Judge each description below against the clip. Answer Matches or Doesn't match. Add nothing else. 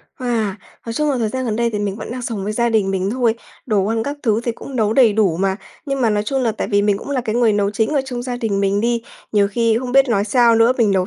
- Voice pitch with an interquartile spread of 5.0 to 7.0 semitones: Doesn't match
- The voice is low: Doesn't match